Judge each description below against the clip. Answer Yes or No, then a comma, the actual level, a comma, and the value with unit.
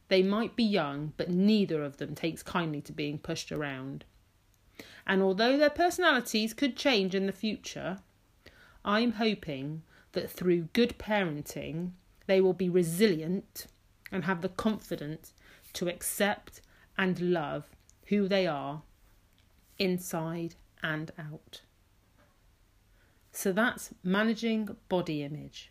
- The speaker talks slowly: Yes, slow, 120 wpm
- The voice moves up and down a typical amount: No, wide, 6.3 semitones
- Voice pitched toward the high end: No, medium, 175 Hz